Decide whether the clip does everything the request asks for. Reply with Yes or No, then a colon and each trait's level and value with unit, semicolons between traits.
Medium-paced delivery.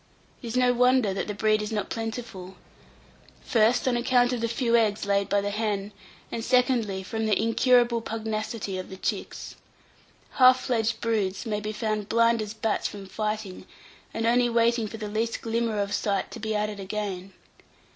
Yes: average, 185 wpm